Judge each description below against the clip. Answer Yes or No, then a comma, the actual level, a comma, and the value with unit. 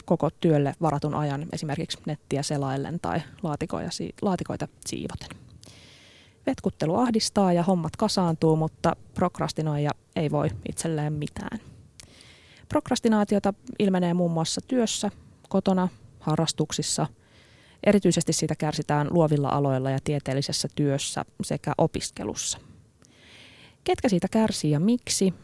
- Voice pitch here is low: No, medium, 160 Hz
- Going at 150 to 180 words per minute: No, average, 105 wpm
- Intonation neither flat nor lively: Yes, average, 4.6 semitones